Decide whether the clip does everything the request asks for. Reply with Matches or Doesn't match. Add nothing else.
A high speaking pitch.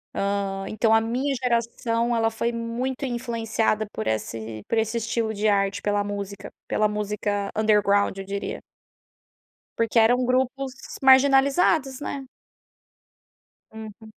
Matches